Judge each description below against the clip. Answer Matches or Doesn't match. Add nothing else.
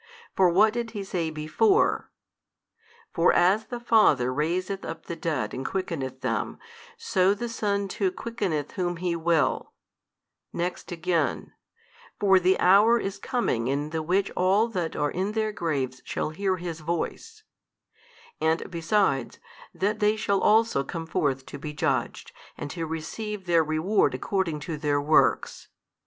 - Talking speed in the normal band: Matches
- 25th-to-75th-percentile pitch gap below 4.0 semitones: Doesn't match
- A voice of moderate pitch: Matches